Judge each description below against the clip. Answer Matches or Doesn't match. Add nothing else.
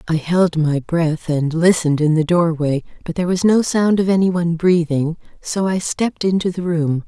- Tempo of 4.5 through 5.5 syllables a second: Matches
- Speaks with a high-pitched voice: Doesn't match